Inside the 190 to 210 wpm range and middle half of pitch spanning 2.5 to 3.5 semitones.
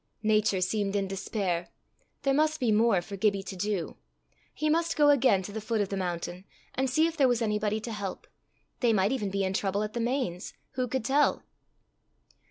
No: average, 200 wpm; average, 4.7 semitones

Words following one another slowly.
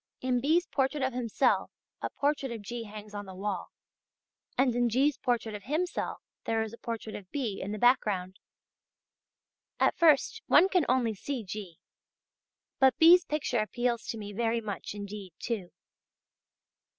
No: average, 160 wpm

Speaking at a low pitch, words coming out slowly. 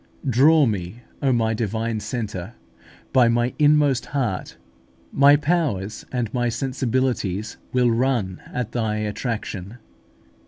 Yes: low, 120 Hz; slow, 120 wpm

